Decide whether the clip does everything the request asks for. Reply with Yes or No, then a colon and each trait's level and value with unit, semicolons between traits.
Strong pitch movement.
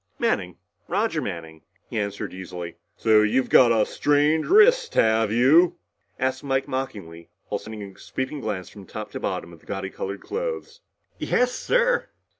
Yes: wide, 7.1 semitones